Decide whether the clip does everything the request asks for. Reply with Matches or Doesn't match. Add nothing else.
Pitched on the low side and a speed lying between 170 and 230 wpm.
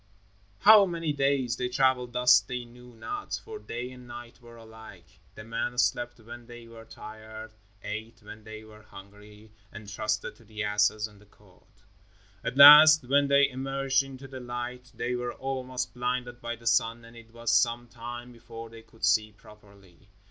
Matches